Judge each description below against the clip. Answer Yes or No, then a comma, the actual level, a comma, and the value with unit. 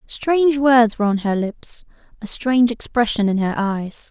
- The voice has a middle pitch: No, high, 230 Hz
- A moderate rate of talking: Yes, average, 175 wpm